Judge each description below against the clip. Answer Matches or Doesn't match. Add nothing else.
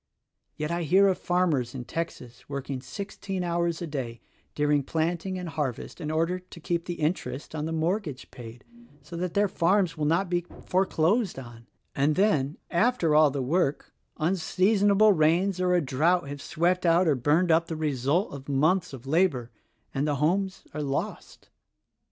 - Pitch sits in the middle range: Matches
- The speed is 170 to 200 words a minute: Matches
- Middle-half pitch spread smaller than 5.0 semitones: Matches